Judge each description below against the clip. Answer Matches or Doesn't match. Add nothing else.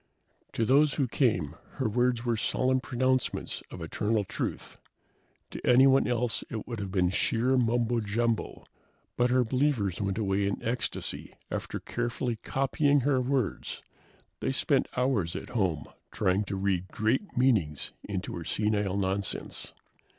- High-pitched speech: Doesn't match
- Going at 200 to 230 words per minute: Doesn't match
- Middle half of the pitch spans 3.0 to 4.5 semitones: Matches